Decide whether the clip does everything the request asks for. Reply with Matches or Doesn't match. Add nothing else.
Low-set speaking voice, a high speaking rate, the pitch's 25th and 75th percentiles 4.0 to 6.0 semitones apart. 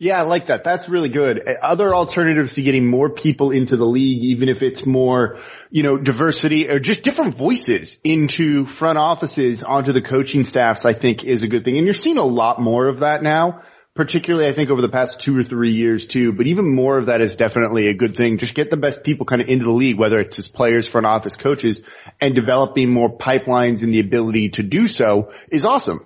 Matches